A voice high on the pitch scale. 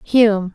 Yes: high, 210 Hz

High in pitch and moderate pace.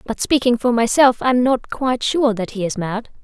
No: high, 240 Hz; fast, 220 wpm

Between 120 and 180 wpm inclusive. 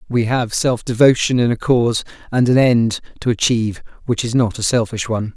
No: average, 200 wpm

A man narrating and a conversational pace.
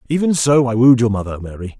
No: male; fast, 235 wpm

